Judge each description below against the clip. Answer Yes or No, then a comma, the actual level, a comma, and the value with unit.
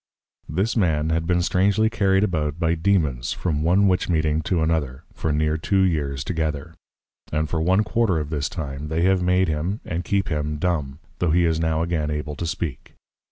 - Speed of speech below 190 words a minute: No, average, 195 wpm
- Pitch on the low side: Yes, very low, 80 Hz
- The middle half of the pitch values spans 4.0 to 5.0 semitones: No, average, 3.3 semitones